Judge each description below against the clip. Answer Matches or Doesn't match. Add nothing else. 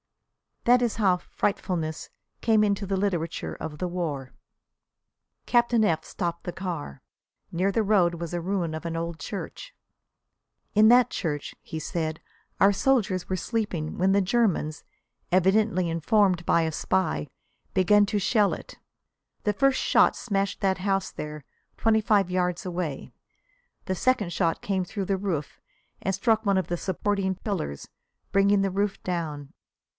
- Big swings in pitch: Doesn't match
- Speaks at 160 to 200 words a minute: Doesn't match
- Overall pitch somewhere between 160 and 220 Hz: Matches